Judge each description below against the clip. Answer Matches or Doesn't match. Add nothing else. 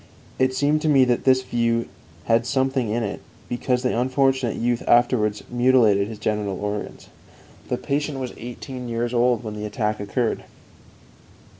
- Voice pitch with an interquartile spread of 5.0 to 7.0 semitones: Doesn't match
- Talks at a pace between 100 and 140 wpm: Doesn't match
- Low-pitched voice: Matches